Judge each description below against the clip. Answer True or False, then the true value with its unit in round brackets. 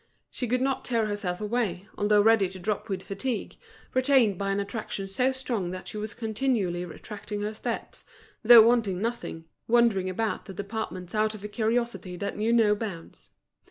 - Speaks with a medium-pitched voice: False (215 Hz)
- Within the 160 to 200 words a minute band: True (175 wpm)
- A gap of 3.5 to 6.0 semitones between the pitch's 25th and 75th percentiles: False (3.1 semitones)